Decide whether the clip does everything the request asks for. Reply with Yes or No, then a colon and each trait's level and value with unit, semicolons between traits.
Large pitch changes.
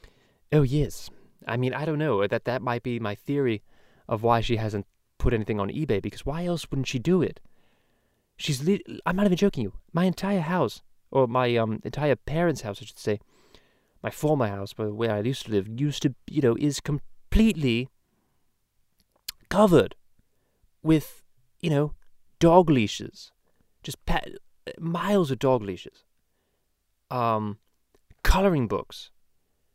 Yes: wide, 6.2 semitones